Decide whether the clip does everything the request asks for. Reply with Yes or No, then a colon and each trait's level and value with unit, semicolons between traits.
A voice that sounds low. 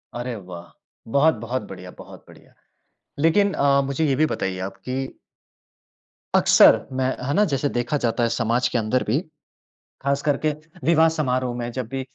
Yes: low, 130 Hz